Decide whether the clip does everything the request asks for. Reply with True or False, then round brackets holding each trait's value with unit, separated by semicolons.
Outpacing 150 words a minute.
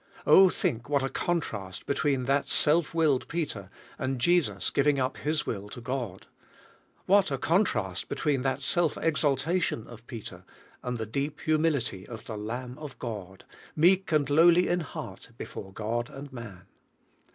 True (160 wpm)